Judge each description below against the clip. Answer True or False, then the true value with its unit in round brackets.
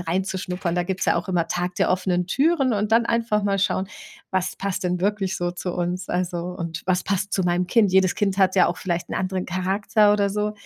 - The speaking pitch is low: False (185 Hz)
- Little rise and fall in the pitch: True (2.1 semitones)